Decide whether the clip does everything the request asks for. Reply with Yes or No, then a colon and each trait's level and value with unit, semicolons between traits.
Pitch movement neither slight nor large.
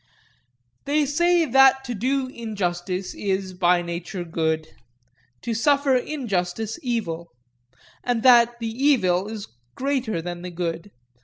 No: wide, 6.7 semitones